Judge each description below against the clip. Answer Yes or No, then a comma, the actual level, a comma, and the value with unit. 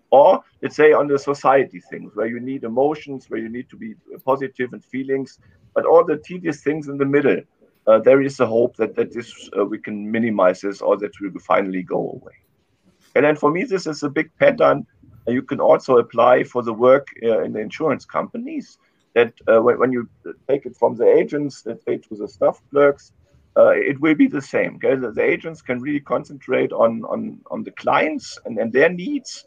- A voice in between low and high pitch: Yes, medium, 145 Hz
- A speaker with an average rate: No, fast, 215 wpm